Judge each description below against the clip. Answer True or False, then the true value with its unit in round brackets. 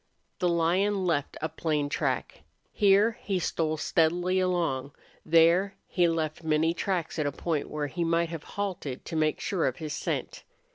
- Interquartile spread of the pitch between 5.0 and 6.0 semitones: False (2.8 semitones)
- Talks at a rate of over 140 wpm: True (165 wpm)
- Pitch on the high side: False (165 Hz)